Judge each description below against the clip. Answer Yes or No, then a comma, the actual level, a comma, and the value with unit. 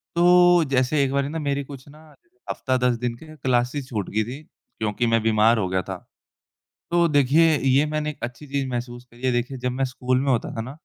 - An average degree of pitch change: Yes, average, 3.3 semitones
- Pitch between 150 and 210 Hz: No, low, 130 Hz